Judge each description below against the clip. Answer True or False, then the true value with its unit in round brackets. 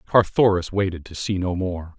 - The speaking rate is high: False (180 wpm)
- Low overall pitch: True (95 Hz)